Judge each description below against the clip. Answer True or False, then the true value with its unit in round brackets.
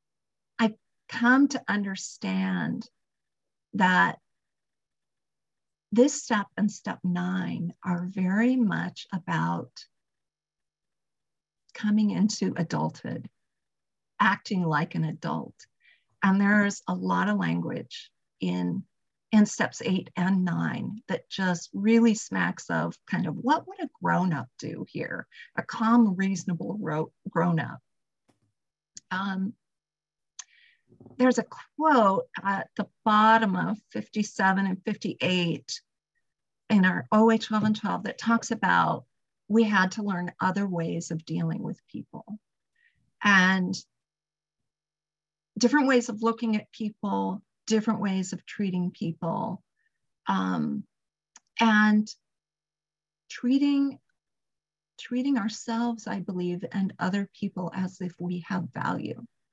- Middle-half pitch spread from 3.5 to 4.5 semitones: True (4.2 semitones)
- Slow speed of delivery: True (110 wpm)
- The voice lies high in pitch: True (195 Hz)